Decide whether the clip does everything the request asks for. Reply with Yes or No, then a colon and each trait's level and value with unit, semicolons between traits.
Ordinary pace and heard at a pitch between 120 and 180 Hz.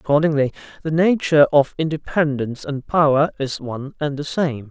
Yes: average, 155 wpm; medium, 145 Hz